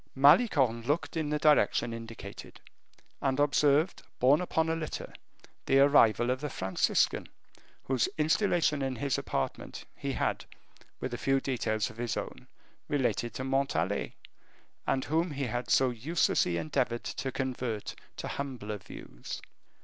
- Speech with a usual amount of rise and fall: Yes, average, 3.8 semitones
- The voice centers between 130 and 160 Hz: Yes, low, 135 Hz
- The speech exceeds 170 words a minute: No, average, 140 wpm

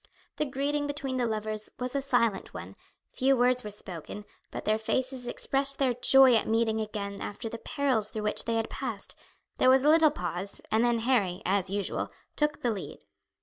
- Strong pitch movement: No, average, 4.0 semitones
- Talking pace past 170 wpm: Yes, average, 190 wpm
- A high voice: Yes, high, 235 Hz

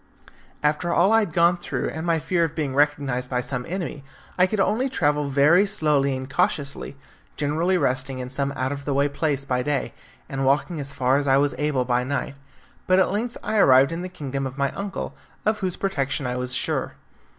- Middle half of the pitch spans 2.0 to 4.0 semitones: No, average, 4.4 semitones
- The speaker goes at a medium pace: No, fast, 210 wpm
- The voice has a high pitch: No, medium, 145 Hz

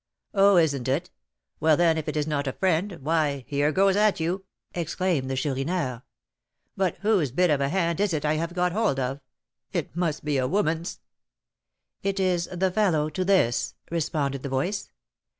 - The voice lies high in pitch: No, medium, 160 Hz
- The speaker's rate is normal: Yes, average, 180 wpm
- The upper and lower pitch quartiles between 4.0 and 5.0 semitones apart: Yes, average, 4.5 semitones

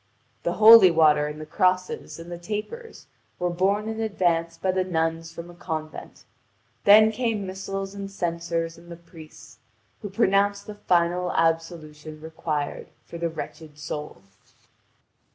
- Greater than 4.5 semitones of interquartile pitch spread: No, average, 3.3 semitones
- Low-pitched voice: No, medium, 175 Hz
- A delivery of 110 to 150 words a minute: Yes, average, 145 wpm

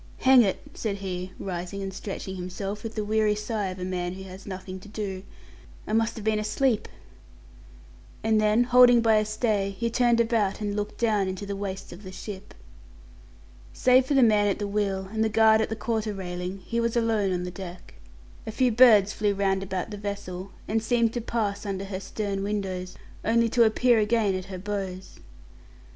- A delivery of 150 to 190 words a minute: No, average, 200 wpm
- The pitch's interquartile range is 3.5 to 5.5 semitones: No, narrow, 2.6 semitones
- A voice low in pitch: No, high, 205 Hz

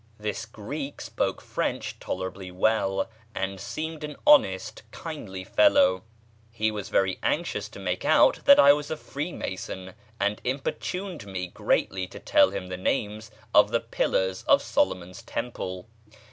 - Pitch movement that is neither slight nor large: No, wide, 7.7 semitones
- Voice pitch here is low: Yes, low, 105 Hz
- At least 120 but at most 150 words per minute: Yes, average, 145 wpm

